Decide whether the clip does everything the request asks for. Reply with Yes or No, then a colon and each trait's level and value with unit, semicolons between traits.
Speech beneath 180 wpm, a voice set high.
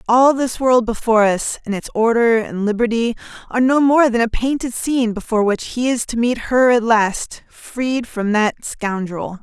No: average, 190 wpm; high, 230 Hz